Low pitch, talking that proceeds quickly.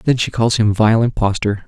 Yes: low, 110 Hz; fast, 215 wpm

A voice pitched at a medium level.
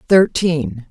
Yes: medium, 150 Hz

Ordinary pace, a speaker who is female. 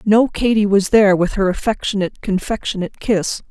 Yes: average, 155 wpm; female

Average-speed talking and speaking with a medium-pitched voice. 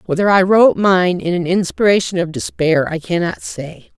Yes: average, 180 wpm; medium, 180 Hz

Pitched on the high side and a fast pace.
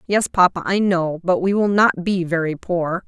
No: medium, 180 Hz; fast, 215 wpm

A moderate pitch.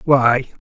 No: low, 130 Hz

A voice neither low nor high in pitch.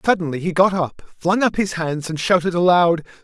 Yes: medium, 175 Hz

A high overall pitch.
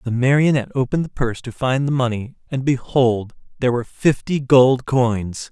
No: low, 125 Hz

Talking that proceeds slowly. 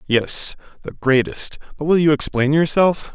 No: average, 155 wpm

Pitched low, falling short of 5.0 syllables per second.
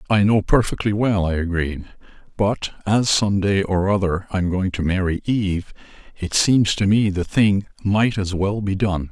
Yes: very low, 95 Hz; 4.5 syllables/s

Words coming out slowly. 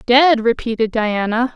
Yes: slow, 115 wpm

